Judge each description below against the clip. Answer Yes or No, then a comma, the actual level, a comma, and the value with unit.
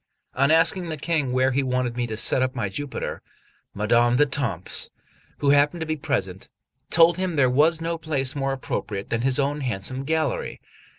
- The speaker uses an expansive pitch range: No, average, 4.2 semitones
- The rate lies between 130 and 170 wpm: No, average, 180 wpm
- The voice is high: No, low, 135 Hz